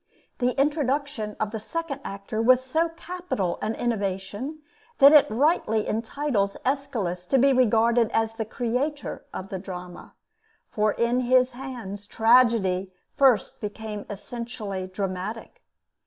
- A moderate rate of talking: No, slow, 125 wpm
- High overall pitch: Yes, high, 230 Hz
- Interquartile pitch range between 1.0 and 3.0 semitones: No, average, 4.5 semitones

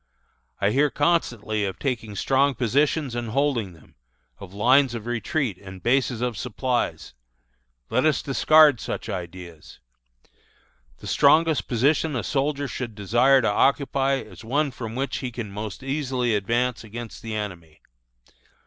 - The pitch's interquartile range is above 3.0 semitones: Yes, average, 4.4 semitones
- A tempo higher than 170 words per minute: No, average, 145 wpm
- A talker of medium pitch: No, low, 120 Hz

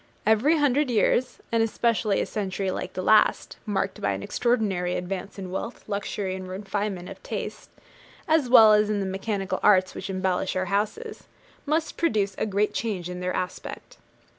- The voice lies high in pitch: Yes, high, 205 Hz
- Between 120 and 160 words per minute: No, average, 170 wpm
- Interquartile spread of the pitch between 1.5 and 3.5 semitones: Yes, average, 3.2 semitones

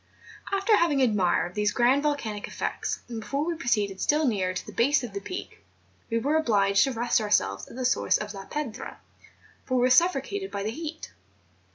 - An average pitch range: No, wide, 6.2 semitones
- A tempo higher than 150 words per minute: Yes, average, 195 wpm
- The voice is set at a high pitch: Yes, high, 240 Hz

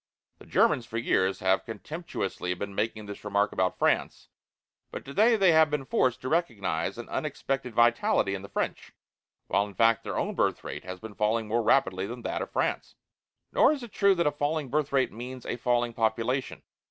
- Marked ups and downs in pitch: Yes, wide, 5.7 semitones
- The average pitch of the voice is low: Yes, low, 120 Hz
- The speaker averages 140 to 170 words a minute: No, average, 195 wpm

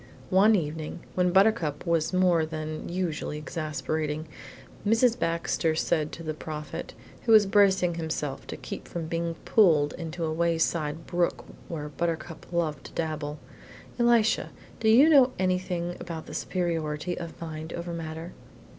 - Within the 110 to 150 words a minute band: Yes, average, 145 wpm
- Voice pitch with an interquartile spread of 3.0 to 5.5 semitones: No, narrow, 2.6 semitones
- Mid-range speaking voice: Yes, medium, 165 Hz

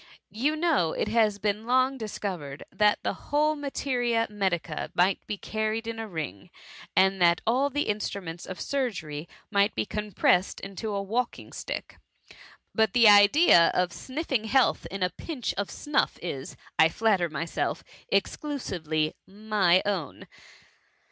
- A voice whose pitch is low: No, high, 210 Hz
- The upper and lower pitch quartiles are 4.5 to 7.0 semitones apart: Yes, average, 5.1 semitones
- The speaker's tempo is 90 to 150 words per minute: Yes, average, 145 wpm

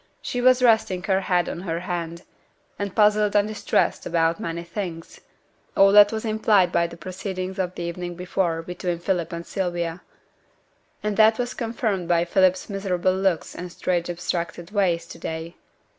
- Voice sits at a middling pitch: Yes, medium, 180 Hz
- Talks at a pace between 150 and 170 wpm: Yes, average, 165 wpm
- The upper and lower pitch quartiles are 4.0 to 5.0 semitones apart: No, average, 3.0 semitones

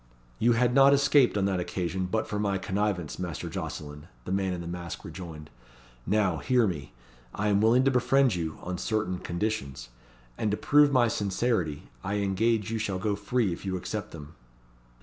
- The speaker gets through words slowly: No, average, 185 wpm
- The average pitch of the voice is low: Yes, low, 100 Hz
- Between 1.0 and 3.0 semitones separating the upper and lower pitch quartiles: No, average, 4.2 semitones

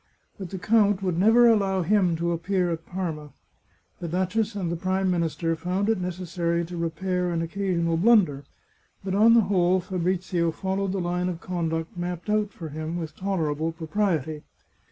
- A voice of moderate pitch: Yes, medium, 180 Hz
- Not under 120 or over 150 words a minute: No, average, 180 wpm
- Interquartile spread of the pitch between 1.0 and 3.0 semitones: Yes, narrow, 2.5 semitones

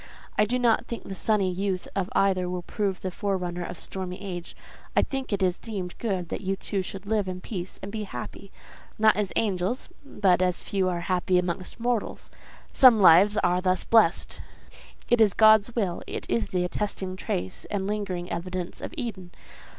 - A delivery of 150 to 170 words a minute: No, average, 180 wpm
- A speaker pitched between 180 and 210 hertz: Yes, high, 190 Hz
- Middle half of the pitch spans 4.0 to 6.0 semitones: No, average, 2.7 semitones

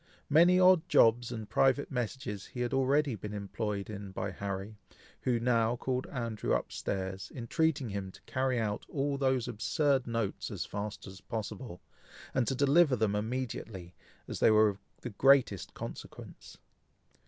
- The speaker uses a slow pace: No, average, 155 wpm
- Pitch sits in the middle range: No, low, 115 Hz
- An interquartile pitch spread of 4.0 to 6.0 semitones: Yes, average, 4.3 semitones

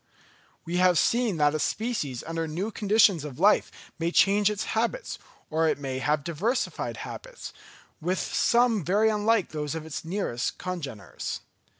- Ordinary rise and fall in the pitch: No, wide, 5.8 semitones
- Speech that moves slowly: No, average, 155 wpm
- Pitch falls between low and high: Yes, medium, 180 Hz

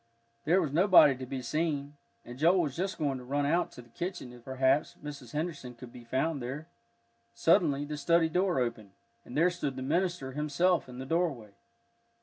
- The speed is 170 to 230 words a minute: Yes, average, 190 wpm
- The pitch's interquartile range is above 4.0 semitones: Yes, average, 4.5 semitones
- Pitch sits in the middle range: Yes, medium, 145 Hz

